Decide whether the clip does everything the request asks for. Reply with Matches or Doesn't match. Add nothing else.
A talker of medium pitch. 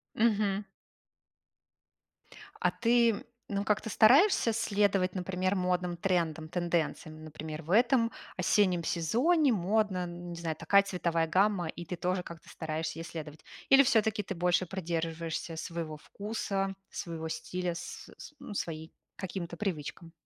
Matches